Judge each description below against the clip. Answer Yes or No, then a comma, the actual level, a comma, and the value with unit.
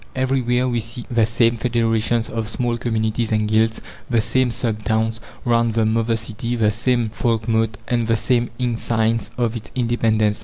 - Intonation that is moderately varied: No, narrow, 1.4 semitones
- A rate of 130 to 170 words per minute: Yes, average, 165 wpm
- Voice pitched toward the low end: Yes, low, 115 Hz